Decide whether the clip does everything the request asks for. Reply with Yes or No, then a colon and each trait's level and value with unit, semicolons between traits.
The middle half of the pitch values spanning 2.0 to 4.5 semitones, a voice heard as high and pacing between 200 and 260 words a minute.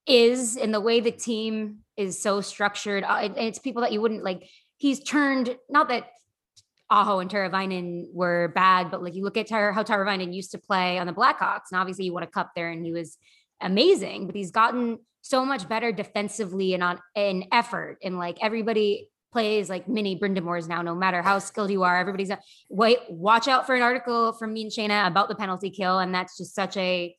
Yes: average, 3.6 semitones; high, 205 Hz; fast, 205 wpm